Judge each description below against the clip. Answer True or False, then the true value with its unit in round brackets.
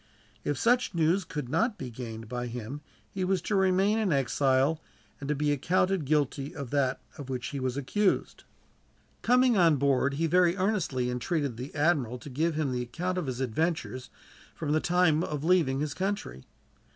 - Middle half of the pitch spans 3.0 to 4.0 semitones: False (5.5 semitones)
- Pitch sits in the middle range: True (150 Hz)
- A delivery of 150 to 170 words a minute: False (180 wpm)